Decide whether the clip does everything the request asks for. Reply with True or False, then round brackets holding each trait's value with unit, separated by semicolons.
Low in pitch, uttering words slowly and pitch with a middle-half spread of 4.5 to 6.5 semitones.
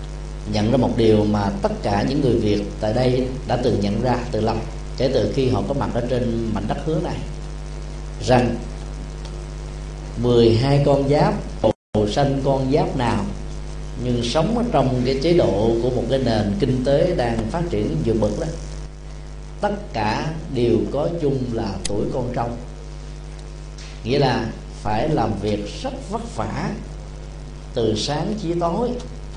True (130 Hz; 160 wpm; 5.2 semitones)